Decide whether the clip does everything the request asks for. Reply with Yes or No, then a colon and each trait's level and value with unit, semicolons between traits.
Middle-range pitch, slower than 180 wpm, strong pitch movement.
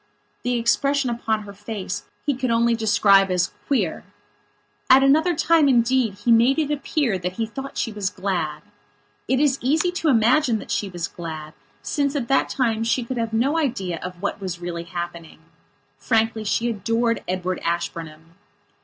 No: high, 225 Hz; average, 170 wpm; wide, 6.0 semitones